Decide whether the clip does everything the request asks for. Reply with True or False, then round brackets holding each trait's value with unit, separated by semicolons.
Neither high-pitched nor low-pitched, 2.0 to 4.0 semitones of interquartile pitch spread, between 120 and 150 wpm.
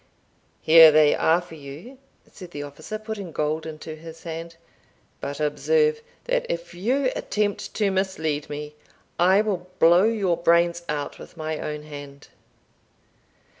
False (170 Hz; 4.4 semitones; 140 wpm)